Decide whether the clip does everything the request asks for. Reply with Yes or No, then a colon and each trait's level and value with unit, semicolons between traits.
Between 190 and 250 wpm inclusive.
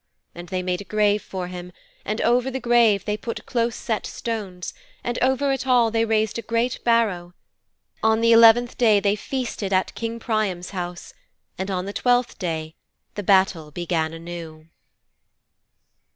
No: average, 165 wpm